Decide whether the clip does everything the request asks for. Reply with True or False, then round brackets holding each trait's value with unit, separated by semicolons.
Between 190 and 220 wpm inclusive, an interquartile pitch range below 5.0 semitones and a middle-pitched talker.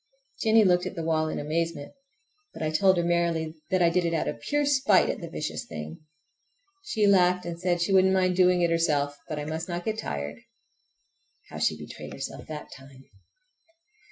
True (195 wpm; 2.9 semitones; 170 Hz)